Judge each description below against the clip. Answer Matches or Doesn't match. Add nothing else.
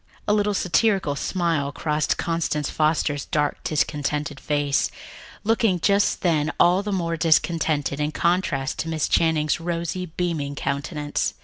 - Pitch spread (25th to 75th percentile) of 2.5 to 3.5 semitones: Matches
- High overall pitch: Doesn't match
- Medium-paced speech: Doesn't match